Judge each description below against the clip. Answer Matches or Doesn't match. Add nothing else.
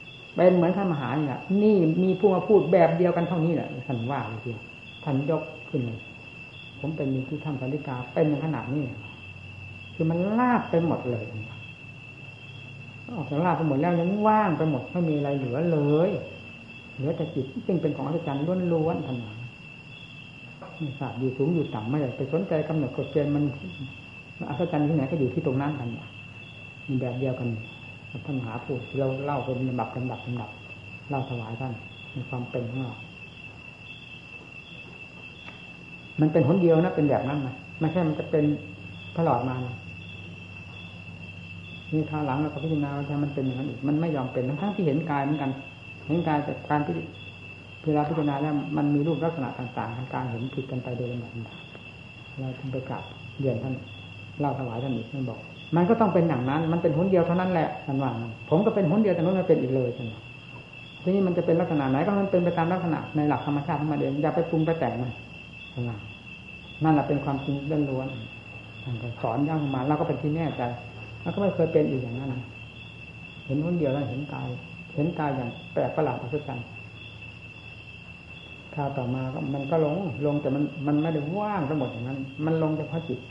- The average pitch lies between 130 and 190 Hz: Matches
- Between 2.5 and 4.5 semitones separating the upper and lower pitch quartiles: Matches